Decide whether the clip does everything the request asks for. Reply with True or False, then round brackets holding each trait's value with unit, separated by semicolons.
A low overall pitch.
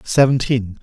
True (120 Hz)